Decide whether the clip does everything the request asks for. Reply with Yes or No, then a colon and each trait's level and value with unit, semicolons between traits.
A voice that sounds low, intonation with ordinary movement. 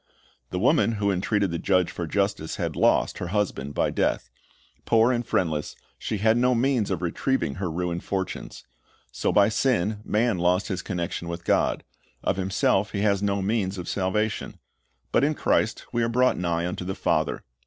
Yes: low, 100 Hz; average, 3.7 semitones